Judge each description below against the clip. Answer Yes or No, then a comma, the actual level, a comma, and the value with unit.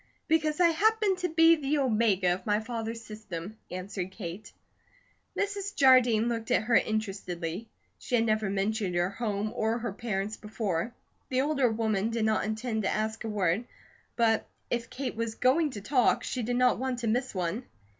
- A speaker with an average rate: Yes, average, 175 wpm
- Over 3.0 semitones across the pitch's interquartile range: Yes, average, 3.4 semitones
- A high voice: Yes, high, 225 Hz